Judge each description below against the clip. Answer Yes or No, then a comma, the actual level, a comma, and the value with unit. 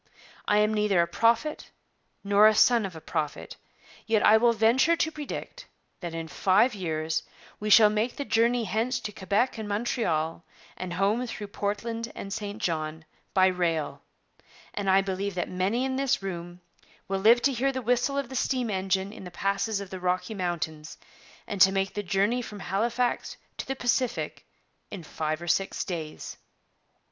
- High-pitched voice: Yes, high, 205 Hz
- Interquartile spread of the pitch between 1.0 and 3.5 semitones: No, average, 4.2 semitones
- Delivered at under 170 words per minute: No, average, 175 wpm